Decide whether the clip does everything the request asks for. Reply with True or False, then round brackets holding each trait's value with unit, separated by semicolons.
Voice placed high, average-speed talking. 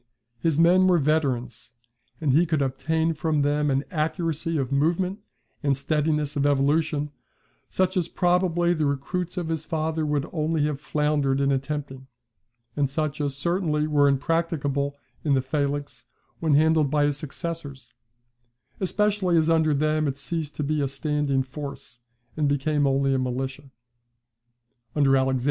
False (150 Hz; 150 wpm)